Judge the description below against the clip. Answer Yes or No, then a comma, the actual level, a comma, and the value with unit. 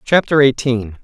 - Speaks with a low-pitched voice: Yes, low, 130 Hz